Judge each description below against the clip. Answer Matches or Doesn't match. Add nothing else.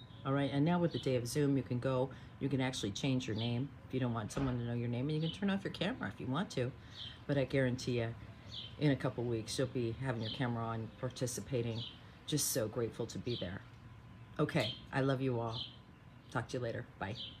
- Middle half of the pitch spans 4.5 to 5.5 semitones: Doesn't match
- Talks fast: Matches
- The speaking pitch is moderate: Doesn't match